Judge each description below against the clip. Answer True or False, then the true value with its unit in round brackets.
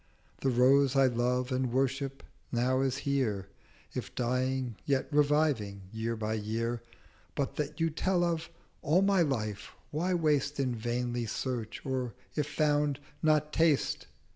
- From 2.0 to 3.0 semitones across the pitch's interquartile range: False (3.6 semitones)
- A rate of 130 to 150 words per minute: True (140 wpm)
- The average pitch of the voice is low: True (130 Hz)